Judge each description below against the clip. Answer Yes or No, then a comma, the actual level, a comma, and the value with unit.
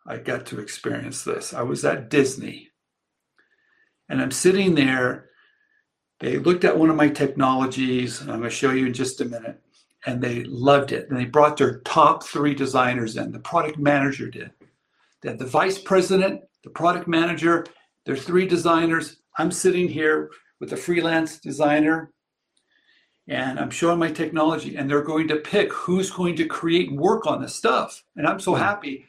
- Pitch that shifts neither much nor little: Yes, average, 4.2 semitones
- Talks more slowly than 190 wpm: Yes, average, 180 wpm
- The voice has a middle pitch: Yes, medium, 155 Hz